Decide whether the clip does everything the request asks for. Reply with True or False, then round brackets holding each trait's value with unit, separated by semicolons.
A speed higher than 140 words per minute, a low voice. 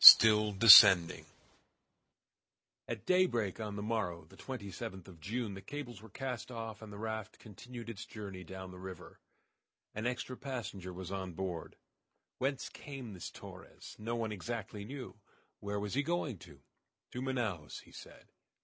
True (155 wpm; 105 Hz)